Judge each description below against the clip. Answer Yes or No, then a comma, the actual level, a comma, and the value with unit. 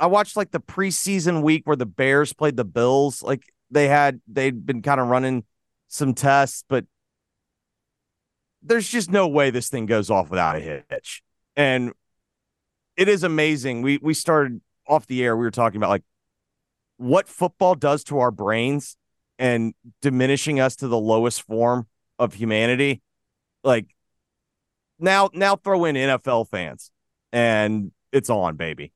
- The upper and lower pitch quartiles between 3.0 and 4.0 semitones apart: No, average, 4.6 semitones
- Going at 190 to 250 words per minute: No, average, 155 wpm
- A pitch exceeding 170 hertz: No, low, 135 Hz